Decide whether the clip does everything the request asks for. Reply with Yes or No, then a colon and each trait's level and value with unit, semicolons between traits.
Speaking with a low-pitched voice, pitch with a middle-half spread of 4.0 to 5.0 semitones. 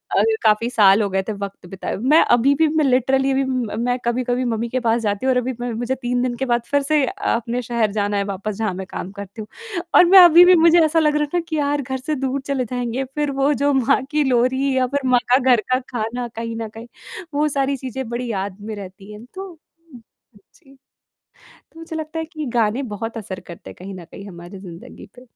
No: very high, 250 Hz; average, 4.3 semitones